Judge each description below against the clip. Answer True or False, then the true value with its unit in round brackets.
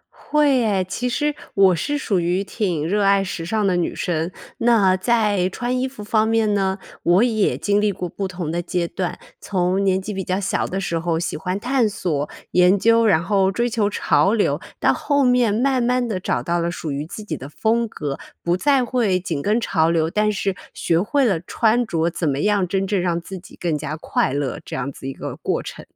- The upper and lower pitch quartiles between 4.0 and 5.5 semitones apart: True (4.3 semitones)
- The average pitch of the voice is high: True (195 Hz)